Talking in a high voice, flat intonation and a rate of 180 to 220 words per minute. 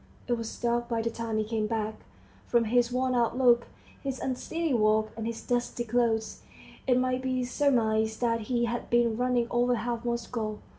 Yes: high, 235 Hz; narrow, 1.7 semitones; average, 185 wpm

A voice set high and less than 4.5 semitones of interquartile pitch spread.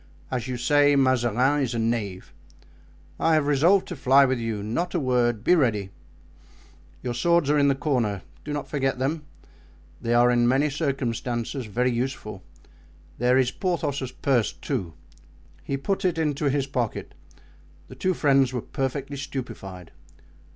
No: low, 130 Hz; average, 3.3 semitones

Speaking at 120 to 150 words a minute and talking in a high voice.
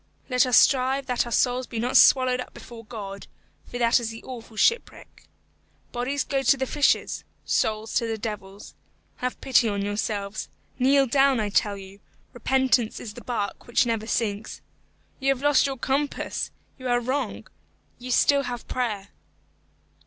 No: average, 165 wpm; high, 245 Hz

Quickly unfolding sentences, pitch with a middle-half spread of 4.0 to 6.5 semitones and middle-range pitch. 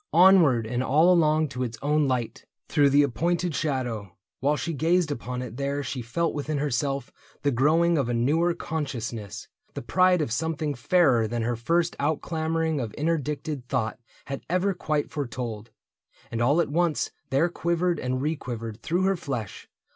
No: average, 170 wpm; average, 4.8 semitones; medium, 145 Hz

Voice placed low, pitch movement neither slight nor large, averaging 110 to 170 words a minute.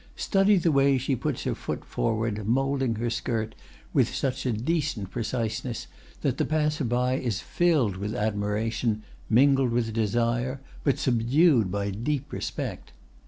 Yes: low, 120 Hz; average, 3.7 semitones; average, 145 wpm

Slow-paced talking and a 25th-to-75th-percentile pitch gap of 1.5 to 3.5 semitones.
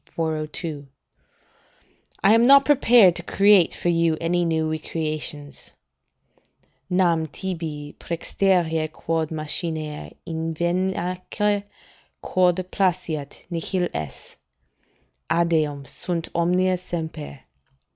Yes: slow, 85 wpm; narrow, 2.6 semitones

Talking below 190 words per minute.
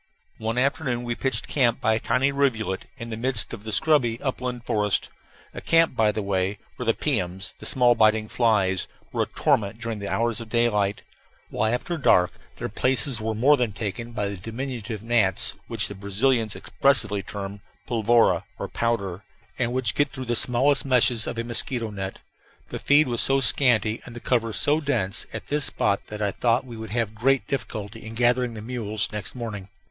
No: average, 195 wpm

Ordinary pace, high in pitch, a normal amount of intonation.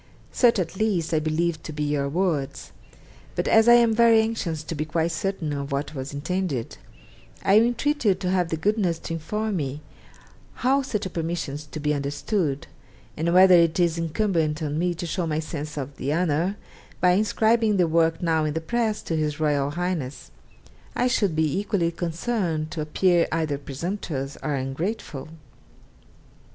No: average, 175 wpm; medium, 165 Hz; average, 4.2 semitones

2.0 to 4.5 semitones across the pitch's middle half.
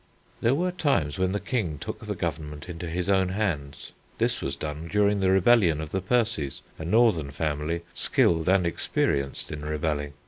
No: average, 4.9 semitones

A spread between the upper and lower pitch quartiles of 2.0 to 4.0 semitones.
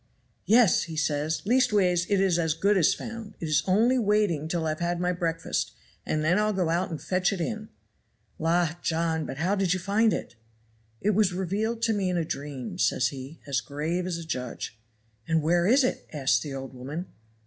No: average, 4.4 semitones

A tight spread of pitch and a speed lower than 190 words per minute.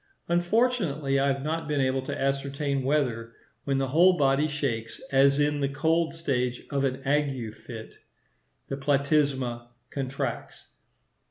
Yes: narrow, 1.9 semitones; average, 140 wpm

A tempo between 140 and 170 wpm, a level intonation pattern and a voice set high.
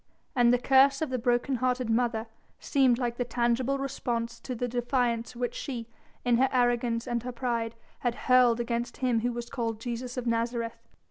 No: average, 185 wpm; narrow, 1.3 semitones; high, 240 Hz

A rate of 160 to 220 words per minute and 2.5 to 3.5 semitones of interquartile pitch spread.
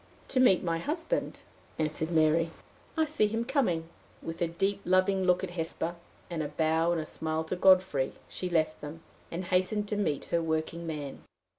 Yes: average, 180 wpm; average, 3.1 semitones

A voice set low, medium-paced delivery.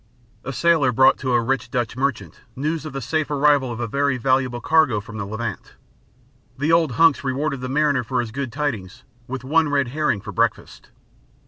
Yes: low, 130 Hz; average, 195 wpm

